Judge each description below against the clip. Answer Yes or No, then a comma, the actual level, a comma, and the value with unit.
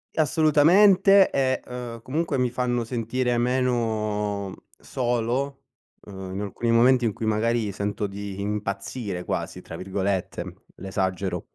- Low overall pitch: Yes, low, 115 Hz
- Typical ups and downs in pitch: Yes, average, 4.1 semitones